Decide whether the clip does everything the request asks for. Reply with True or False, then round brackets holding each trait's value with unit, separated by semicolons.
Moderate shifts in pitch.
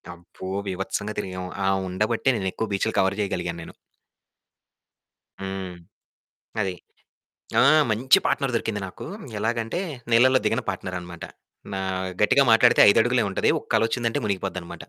True (3.4 semitones)